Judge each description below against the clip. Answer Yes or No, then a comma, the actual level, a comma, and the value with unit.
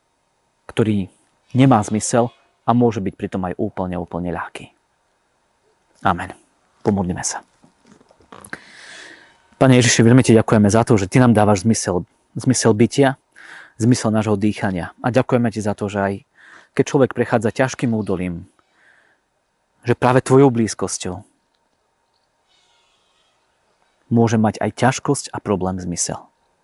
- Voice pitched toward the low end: Yes, low, 115 Hz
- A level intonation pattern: No, average, 3.8 semitones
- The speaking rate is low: No, average, 120 wpm